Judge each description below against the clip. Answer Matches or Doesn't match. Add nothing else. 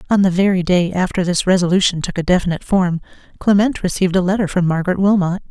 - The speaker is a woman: Matches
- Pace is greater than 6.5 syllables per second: Matches